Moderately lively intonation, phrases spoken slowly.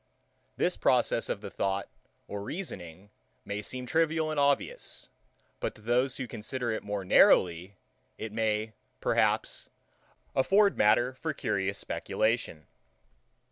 Yes: average, 4.7 semitones; slow, 125 wpm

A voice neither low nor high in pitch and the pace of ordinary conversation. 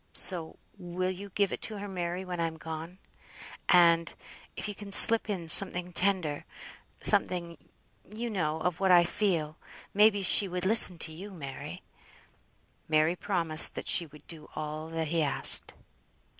Yes: medium, 175 Hz; average, 160 wpm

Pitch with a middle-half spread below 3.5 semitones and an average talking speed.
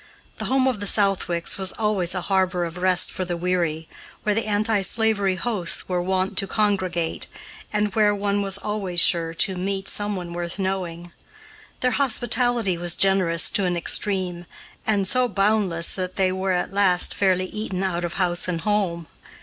Yes: narrow, 2.6 semitones; average, 175 wpm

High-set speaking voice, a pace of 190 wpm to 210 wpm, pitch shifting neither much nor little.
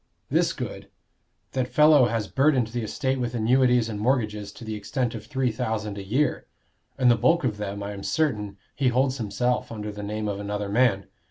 No: low, 115 Hz; average, 195 wpm; average, 3.7 semitones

